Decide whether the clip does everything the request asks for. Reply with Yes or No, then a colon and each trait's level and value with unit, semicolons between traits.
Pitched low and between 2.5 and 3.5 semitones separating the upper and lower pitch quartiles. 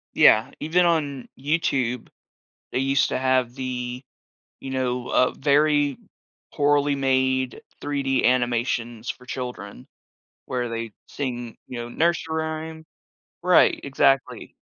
Yes: low, 130 Hz; average, 2.8 semitones